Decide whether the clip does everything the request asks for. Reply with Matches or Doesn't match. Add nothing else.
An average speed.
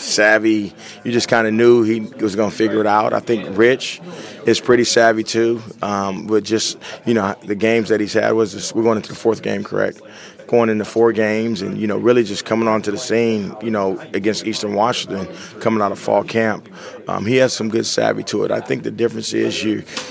Doesn't match